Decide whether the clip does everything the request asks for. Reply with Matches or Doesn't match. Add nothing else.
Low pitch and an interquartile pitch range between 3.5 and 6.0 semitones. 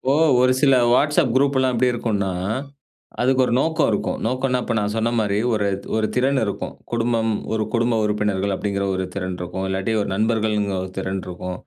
Matches